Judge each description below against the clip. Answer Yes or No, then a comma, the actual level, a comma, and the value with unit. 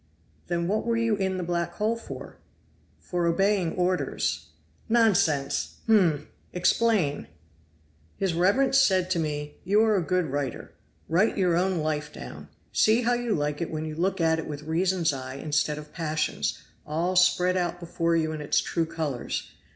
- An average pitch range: Yes, average, 3.7 semitones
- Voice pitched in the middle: Yes, medium, 175 Hz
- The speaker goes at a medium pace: Yes, average, 165 wpm